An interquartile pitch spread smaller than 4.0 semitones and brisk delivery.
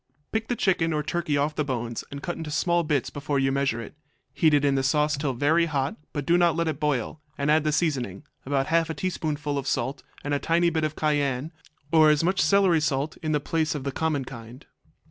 Yes: average, 2.7 semitones; fast, 235 wpm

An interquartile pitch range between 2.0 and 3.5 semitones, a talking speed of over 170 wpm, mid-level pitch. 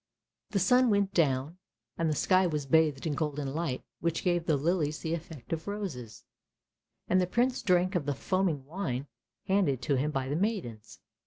No: average, 4.7 semitones; average, 180 wpm; medium, 160 Hz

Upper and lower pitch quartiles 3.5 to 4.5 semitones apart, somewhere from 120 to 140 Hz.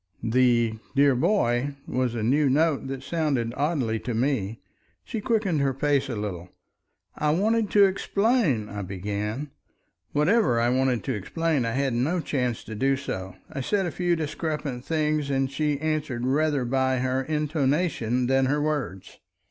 Yes: average, 4.2 semitones; low, 135 Hz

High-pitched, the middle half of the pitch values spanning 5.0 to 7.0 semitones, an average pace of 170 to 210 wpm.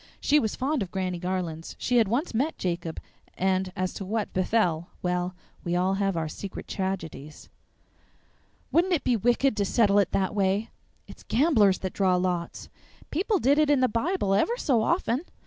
Yes: high, 200 Hz; wide, 5.4 semitones; average, 180 wpm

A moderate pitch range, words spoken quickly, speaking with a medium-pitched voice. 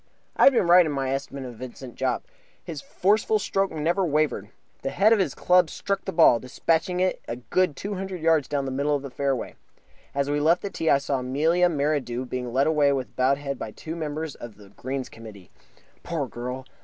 Yes: average, 4.6 semitones; fast, 215 wpm; medium, 145 Hz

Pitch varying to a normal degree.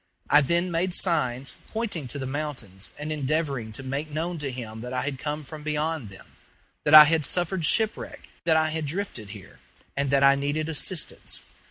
Yes: average, 3.4 semitones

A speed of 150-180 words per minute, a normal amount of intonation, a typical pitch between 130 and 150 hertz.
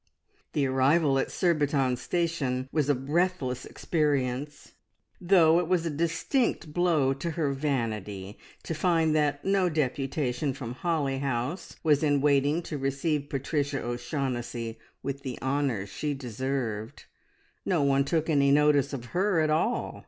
No: average, 140 wpm; average, 3.3 semitones; medium, 140 Hz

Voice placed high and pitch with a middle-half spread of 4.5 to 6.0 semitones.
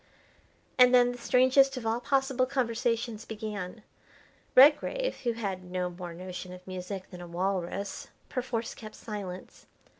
Yes: high, 220 Hz; wide, 5.4 semitones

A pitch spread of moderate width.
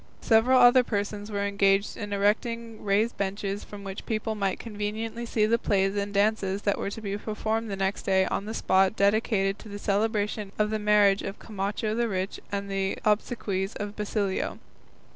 No: narrow, 1.6 semitones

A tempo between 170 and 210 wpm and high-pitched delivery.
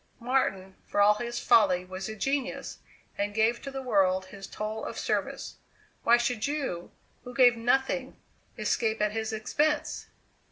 No: average, 155 wpm; high, 225 Hz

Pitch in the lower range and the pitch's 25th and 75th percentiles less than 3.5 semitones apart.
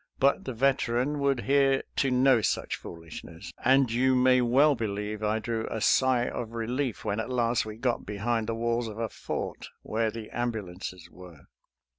Yes: low, 115 Hz; average, 3.1 semitones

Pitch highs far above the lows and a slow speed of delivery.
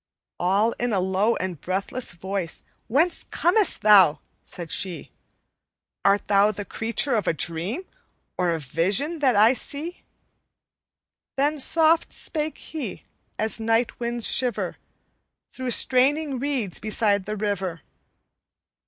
Yes: wide, 6.0 semitones; slow, 125 wpm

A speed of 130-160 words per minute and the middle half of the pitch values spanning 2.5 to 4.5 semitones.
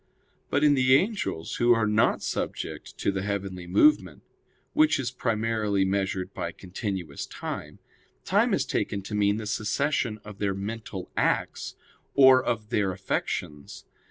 Yes: average, 145 wpm; average, 3.8 semitones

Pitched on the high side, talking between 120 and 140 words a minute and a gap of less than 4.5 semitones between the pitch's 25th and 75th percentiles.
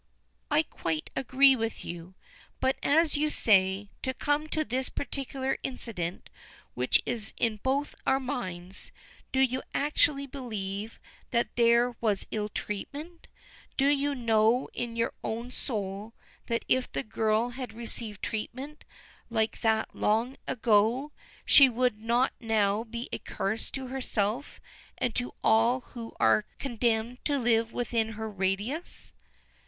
Yes: high, 235 Hz; slow, 135 wpm; average, 3.5 semitones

